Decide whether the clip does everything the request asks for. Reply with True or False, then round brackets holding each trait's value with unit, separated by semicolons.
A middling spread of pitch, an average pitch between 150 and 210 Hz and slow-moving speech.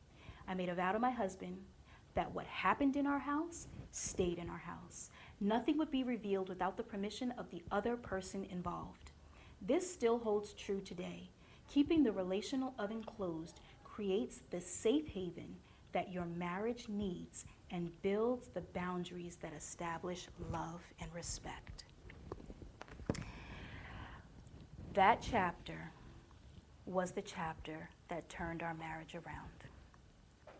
True (4.2 semitones; 185 Hz; 130 wpm)